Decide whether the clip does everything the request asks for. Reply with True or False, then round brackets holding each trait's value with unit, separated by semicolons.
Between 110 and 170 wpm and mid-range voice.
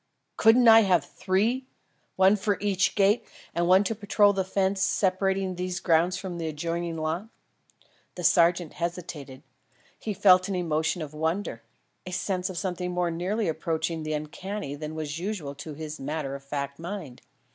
True (165 wpm; 180 Hz)